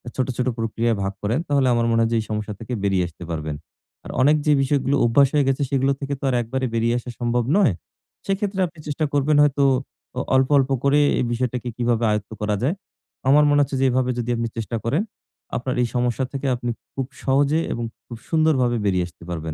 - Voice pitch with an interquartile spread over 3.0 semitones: Yes, average, 3.5 semitones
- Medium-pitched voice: No, low, 125 Hz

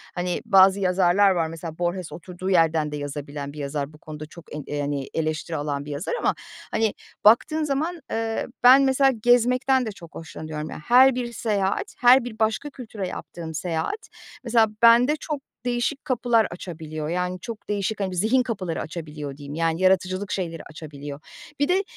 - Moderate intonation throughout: No, wide, 7.0 semitones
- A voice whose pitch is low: No, medium, 185 Hz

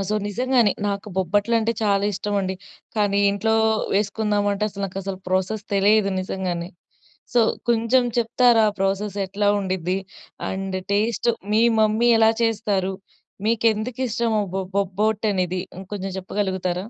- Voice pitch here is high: Yes, high, 205 Hz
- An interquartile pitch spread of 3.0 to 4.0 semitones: No, narrow, 2.5 semitones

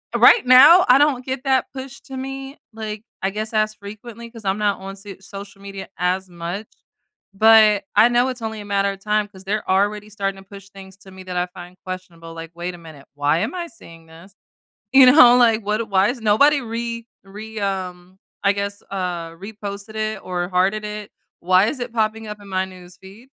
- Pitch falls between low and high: No, high, 205 Hz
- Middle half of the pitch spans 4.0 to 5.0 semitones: No, average, 3.0 semitones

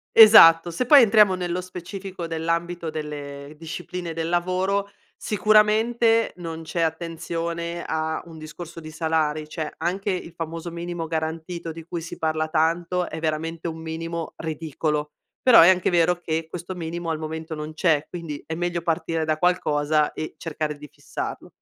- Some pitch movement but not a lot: No, narrow, 1.9 semitones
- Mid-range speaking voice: Yes, medium, 165 Hz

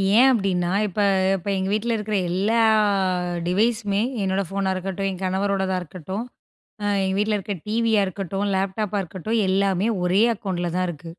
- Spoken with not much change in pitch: Yes, narrow, 2.1 semitones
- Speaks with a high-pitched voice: Yes, high, 195 Hz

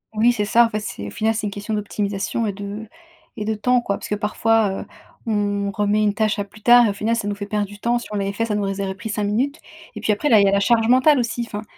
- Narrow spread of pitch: Yes, narrow, 1.9 semitones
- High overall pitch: Yes, high, 210 Hz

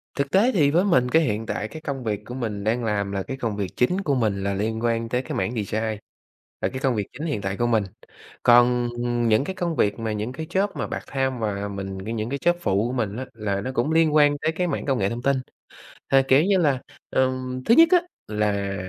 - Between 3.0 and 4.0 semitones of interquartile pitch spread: No, average, 5.1 semitones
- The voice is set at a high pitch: No, low, 120 Hz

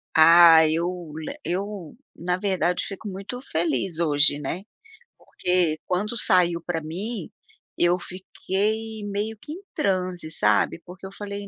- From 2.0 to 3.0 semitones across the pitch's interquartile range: No, average, 3.5 semitones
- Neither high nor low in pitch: Yes, medium, 180 Hz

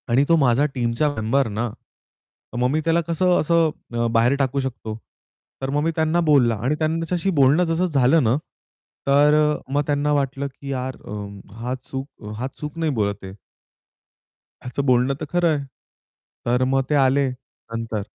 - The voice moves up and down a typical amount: Yes, average, 4.0 semitones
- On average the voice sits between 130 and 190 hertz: Yes, low, 135 Hz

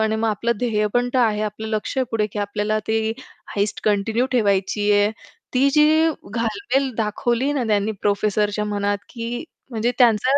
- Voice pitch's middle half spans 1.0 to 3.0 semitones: Yes, narrow, 2.6 semitones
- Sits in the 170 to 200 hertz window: No, high, 220 Hz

